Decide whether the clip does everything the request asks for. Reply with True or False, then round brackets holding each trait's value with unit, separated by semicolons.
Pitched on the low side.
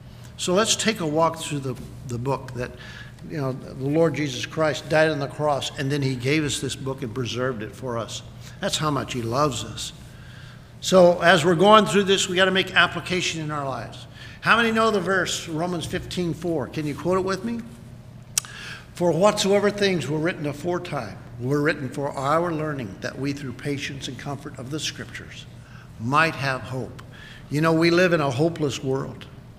False (145 Hz)